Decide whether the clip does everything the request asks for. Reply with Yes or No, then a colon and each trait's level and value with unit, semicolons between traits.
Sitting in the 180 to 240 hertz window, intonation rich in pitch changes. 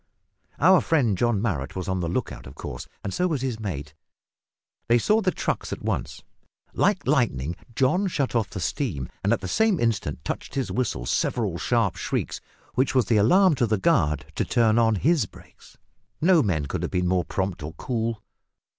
No: low, 110 Hz; wide, 6.7 semitones